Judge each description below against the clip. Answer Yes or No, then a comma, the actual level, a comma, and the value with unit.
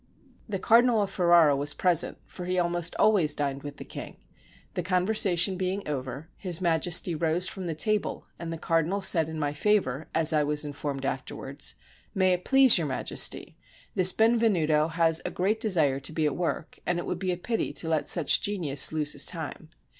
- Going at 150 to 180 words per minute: No, average, 195 wpm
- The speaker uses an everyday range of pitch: Yes, average, 3.7 semitones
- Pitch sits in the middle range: Yes, medium, 170 Hz